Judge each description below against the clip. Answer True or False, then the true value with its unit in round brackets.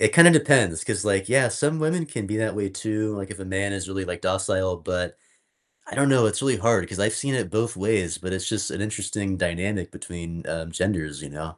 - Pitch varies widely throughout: False (3.3 semitones)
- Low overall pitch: True (100 Hz)